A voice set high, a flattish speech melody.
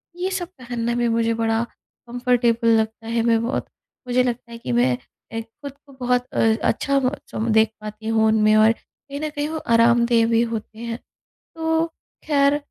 Yes: high, 235 Hz; narrow, 2.2 semitones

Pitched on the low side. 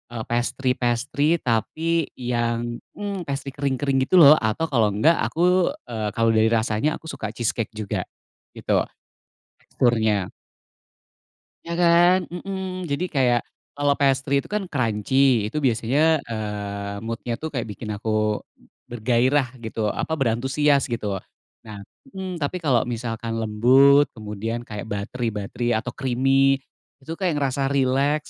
Yes: low, 125 Hz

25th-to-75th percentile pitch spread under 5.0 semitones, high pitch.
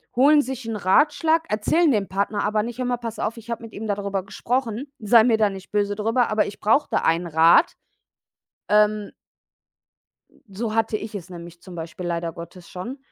Yes: average, 3.6 semitones; high, 215 Hz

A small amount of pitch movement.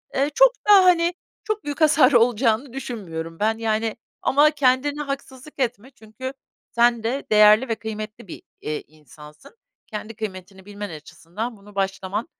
No: average, 4.9 semitones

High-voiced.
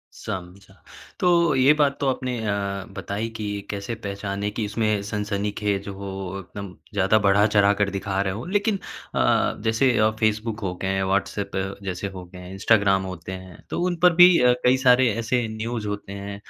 No: low, 105 Hz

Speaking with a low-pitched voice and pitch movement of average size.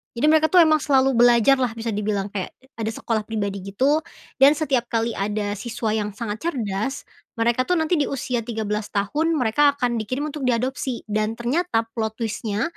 No: high, 235 Hz; average, 4.2 semitones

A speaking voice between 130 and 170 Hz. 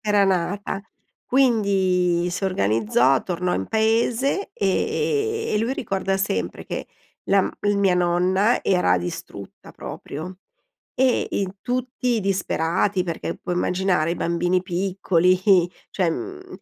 No: high, 190 Hz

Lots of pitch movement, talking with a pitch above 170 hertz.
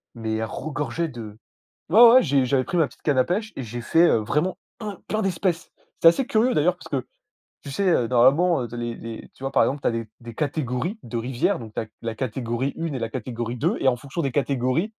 No: wide, 6.0 semitones; low, 135 Hz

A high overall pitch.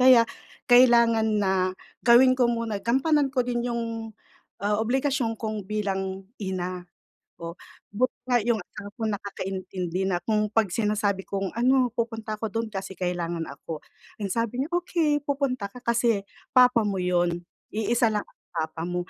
Yes: high, 220 Hz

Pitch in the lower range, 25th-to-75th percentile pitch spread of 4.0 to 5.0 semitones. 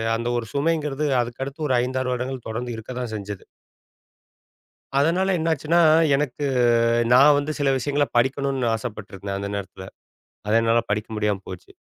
Yes: low, 125 Hz; average, 4.7 semitones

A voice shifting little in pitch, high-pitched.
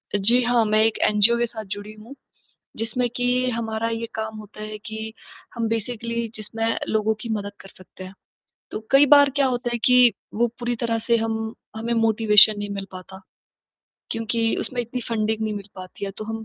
Yes: narrow, 1.8 semitones; high, 225 Hz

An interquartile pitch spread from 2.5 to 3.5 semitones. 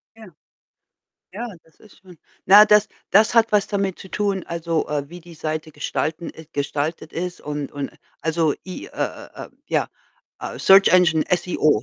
No: average, 4.0 semitones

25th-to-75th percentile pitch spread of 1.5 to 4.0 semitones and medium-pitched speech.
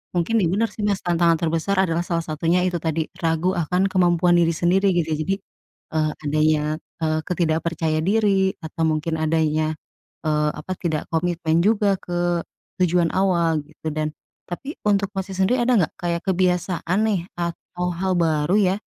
Yes: average, 2.9 semitones; medium, 175 Hz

